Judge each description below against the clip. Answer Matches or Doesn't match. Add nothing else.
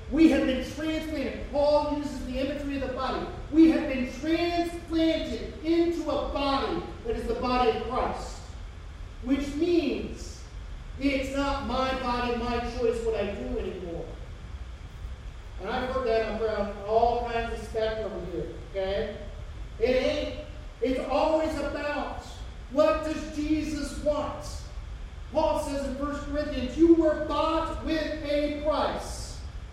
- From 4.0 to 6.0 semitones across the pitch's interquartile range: Matches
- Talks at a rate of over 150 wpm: Doesn't match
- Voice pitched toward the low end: Doesn't match